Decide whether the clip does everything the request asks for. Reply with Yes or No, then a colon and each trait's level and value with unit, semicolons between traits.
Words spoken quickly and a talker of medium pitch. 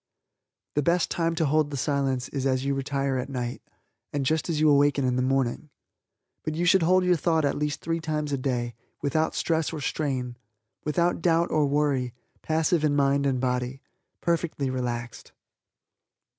No: average, 175 wpm; medium, 145 Hz